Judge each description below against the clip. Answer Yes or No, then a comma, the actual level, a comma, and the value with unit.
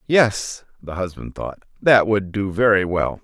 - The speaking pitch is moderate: No, low, 100 Hz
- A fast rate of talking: No, average, 165 wpm